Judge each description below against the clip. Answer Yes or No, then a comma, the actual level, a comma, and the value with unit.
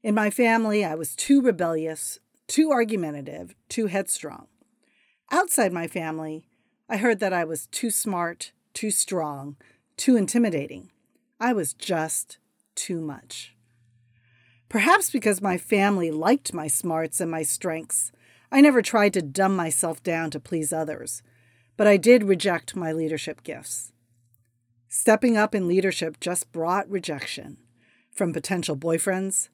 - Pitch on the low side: No, medium, 170 Hz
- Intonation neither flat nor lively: No, wide, 5.7 semitones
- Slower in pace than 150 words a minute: Yes, slow, 135 wpm